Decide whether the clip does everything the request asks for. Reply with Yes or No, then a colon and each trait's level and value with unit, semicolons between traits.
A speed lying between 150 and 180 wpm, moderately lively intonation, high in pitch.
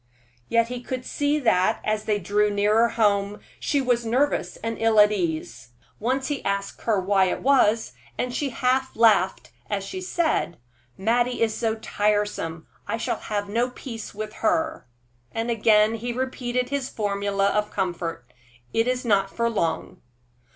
Yes: average, 160 wpm; average, 3.4 semitones; high, 220 Hz